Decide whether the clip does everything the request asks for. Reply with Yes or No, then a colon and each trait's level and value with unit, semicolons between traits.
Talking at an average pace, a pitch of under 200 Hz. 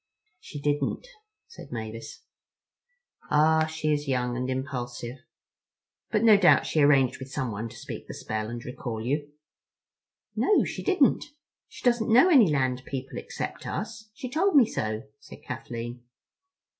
Yes: average, 145 wpm; medium, 140 Hz